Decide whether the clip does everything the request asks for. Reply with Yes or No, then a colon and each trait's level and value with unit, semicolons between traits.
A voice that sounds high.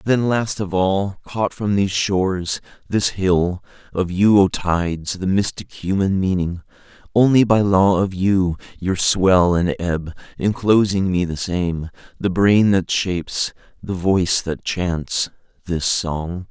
No: very low, 95 Hz